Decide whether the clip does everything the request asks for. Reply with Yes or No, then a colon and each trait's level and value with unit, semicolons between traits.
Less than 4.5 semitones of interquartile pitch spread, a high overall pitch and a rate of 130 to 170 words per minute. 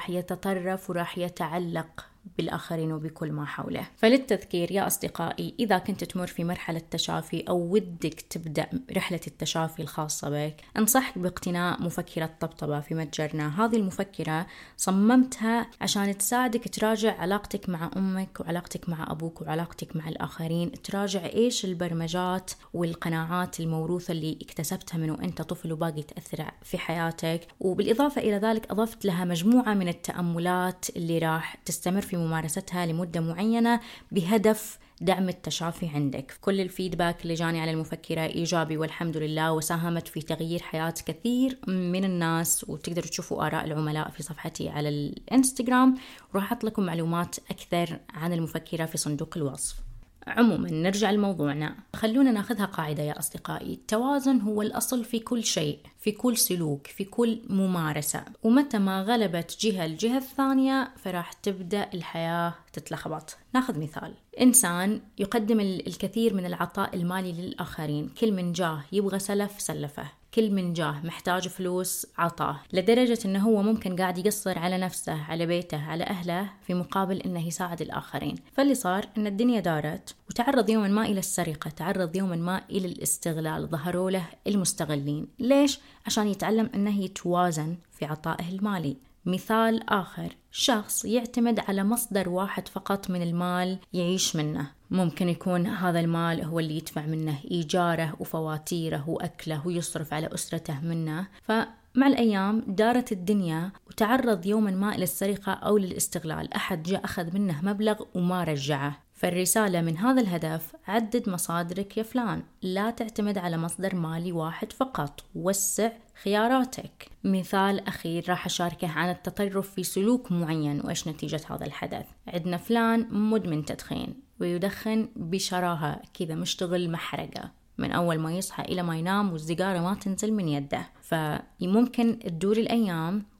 No: average, 4.0 semitones; medium, 180 Hz; fast, 135 wpm